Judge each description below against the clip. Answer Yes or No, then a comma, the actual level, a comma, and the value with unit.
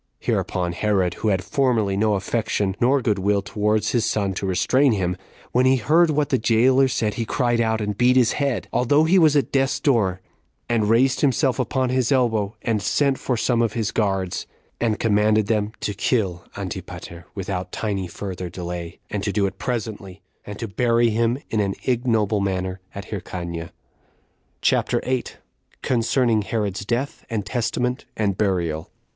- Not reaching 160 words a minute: No, average, 170 wpm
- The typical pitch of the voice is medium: No, low, 110 Hz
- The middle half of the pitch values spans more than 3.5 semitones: Yes, average, 4.0 semitones